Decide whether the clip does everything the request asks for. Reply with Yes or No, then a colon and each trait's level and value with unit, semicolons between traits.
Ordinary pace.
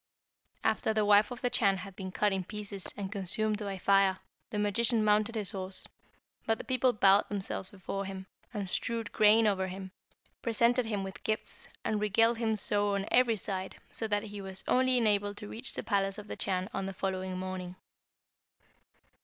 Yes: average, 185 wpm